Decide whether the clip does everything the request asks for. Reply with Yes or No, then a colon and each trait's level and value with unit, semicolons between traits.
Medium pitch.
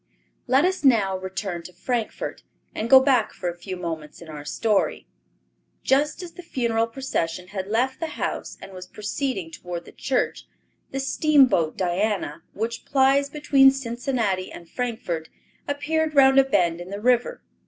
No: high, 230 Hz